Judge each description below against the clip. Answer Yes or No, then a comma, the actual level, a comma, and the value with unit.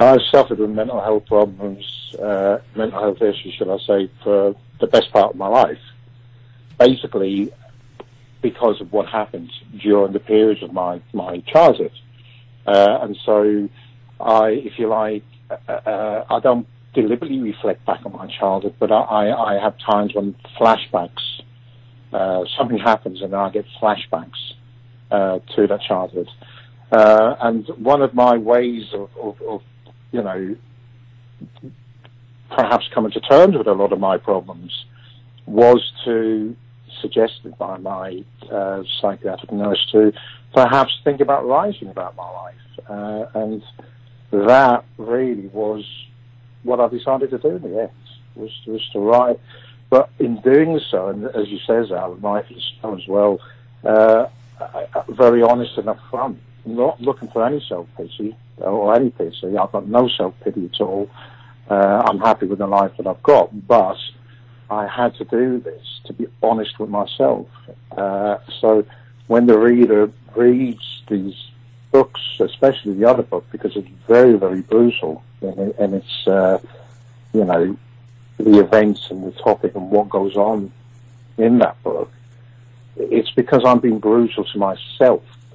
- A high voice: No, low, 120 Hz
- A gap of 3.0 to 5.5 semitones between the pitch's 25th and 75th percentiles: No, narrow, 2.5 semitones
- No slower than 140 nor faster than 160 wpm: Yes, average, 150 wpm